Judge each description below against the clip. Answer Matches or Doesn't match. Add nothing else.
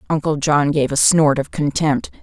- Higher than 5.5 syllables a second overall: Doesn't match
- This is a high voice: Doesn't match